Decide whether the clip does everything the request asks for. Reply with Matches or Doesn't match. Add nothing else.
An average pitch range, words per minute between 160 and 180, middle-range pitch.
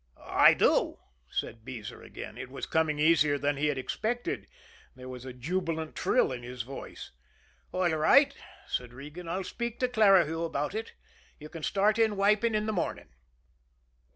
Doesn't match